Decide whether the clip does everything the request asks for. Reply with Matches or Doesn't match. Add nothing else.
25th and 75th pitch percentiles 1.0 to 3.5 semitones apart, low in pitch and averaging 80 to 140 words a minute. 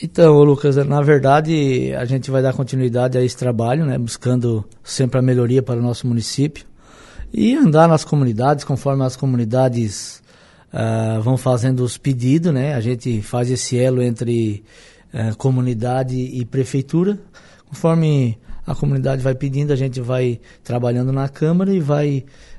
Doesn't match